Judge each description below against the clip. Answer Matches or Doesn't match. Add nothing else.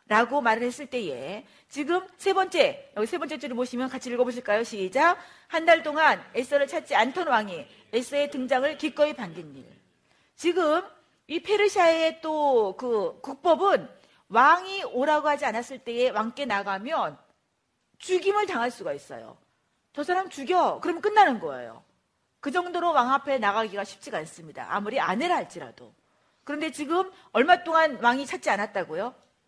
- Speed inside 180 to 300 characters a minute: Doesn't match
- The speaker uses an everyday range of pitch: Doesn't match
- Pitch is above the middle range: Matches